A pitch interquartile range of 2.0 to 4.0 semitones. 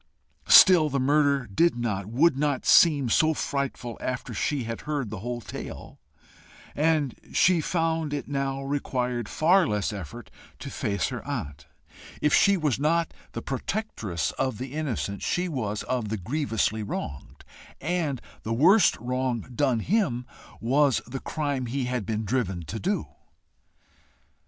No: average, 5.1 semitones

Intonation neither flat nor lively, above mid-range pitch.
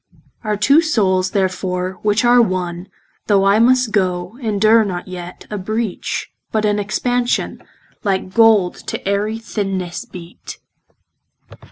Yes: average, 3.2 semitones; high, 205 Hz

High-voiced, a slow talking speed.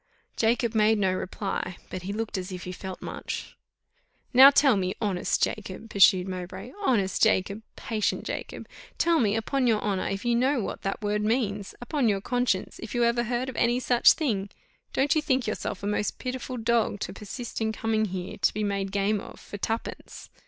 No: high, 215 Hz; average, 195 wpm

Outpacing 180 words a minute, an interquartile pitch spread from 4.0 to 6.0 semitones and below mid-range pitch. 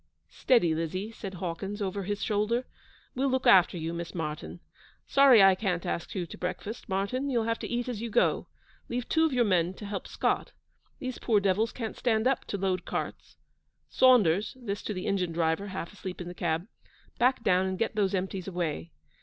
No: average, 195 wpm; average, 4.3 semitones; high, 195 Hz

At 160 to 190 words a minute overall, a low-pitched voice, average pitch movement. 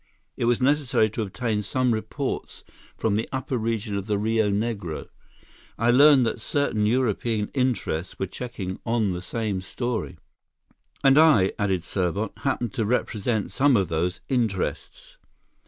No: average, 145 wpm; low, 110 Hz; average, 3.9 semitones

